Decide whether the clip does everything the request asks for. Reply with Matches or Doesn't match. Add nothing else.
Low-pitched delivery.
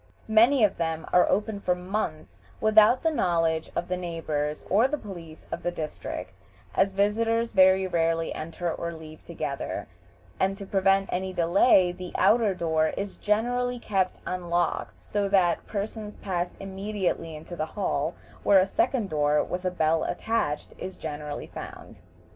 Doesn't match